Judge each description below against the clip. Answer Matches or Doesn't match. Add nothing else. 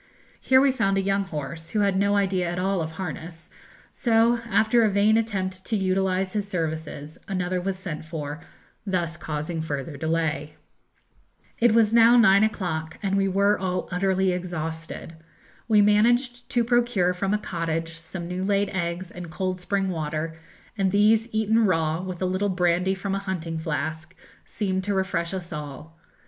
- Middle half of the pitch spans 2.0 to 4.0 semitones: Matches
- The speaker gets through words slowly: Doesn't match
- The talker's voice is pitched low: Doesn't match